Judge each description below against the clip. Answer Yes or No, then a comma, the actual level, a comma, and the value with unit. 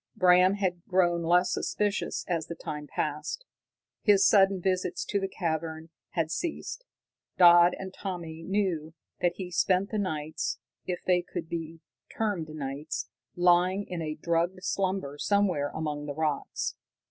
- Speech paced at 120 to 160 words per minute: Yes, average, 145 wpm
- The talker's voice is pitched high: No, medium, 175 Hz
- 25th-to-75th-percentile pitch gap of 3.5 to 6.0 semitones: No, average, 3.0 semitones